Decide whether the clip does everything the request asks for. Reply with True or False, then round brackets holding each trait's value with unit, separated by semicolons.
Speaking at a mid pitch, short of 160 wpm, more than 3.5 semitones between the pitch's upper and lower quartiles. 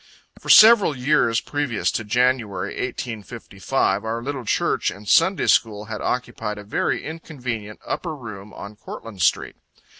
False (115 Hz; 140 wpm; 4.5 semitones)